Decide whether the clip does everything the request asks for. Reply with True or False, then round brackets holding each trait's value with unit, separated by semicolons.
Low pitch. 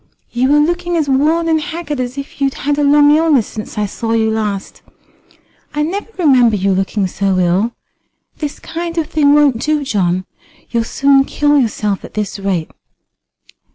False (270 Hz)